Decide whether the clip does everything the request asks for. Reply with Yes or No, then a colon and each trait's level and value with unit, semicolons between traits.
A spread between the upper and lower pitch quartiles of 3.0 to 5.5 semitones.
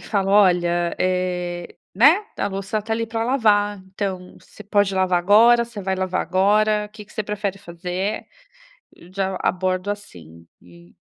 No: narrow, 2.5 semitones